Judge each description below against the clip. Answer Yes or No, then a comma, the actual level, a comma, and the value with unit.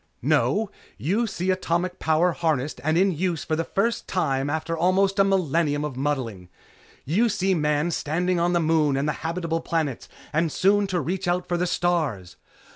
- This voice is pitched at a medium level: Yes, medium, 170 Hz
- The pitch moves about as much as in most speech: Yes, average, 3.5 semitones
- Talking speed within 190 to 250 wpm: No, average, 180 wpm